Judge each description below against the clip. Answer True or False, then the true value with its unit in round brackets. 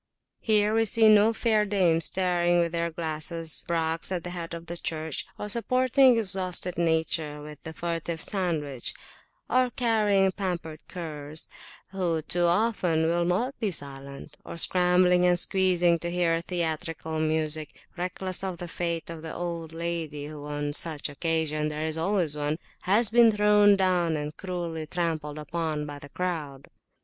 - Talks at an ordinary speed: True (155 wpm)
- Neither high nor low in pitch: True (170 Hz)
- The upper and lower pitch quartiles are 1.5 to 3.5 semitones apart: True (2.9 semitones)